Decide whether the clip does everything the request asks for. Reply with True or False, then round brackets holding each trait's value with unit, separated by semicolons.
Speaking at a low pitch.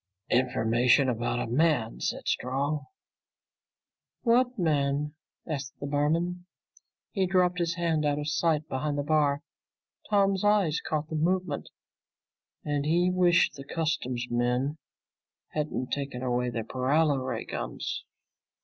False (150 Hz)